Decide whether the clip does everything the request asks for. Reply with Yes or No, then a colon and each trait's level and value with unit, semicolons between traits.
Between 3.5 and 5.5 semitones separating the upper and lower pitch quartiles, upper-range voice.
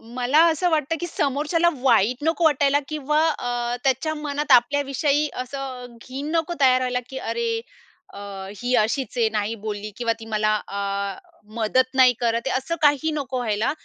Yes: average, 4.0 semitones; very high, 260 Hz